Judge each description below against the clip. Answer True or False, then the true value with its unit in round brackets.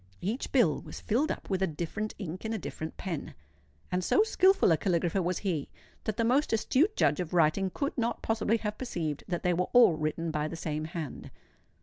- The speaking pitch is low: False (185 Hz)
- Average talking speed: False (210 wpm)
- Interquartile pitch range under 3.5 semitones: False (5.6 semitones)